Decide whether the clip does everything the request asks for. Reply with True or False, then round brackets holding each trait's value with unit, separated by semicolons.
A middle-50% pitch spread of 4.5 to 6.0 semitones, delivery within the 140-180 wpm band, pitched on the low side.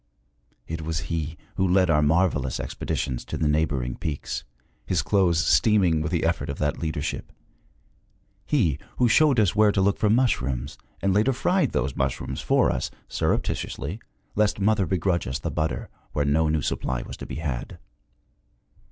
True (5.0 semitones; 165 wpm; 80 Hz)